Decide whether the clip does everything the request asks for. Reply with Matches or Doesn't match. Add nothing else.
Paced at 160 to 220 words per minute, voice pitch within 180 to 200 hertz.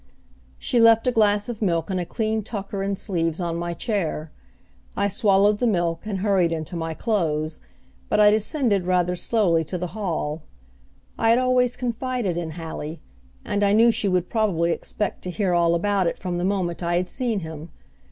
Matches